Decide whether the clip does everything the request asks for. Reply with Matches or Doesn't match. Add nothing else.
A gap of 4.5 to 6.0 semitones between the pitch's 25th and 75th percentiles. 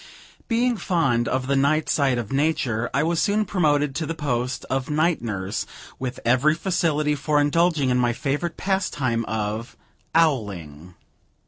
Matches